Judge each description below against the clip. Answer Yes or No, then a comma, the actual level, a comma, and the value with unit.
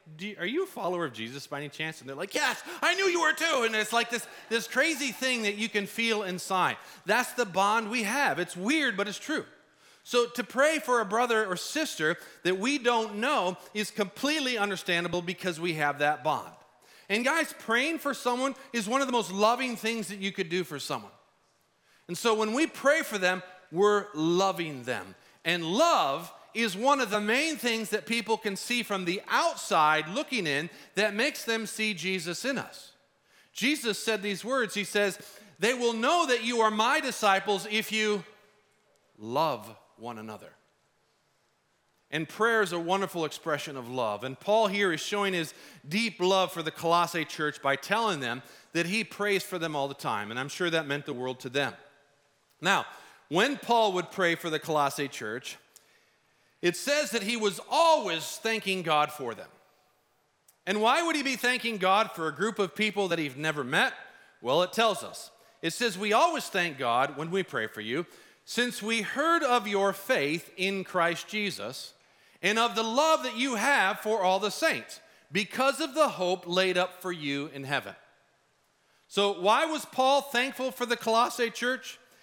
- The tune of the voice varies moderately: No, wide, 5.7 semitones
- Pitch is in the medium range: No, high, 205 Hz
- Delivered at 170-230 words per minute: Yes, average, 190 wpm